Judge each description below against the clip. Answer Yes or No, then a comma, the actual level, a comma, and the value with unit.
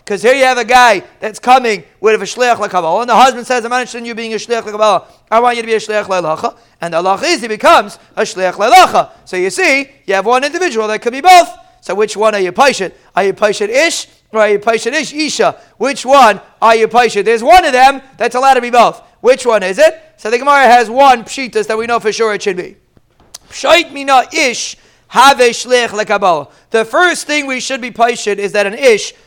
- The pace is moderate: No, fast, 230 wpm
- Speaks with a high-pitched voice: Yes, high, 245 Hz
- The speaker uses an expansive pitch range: No, average, 4.5 semitones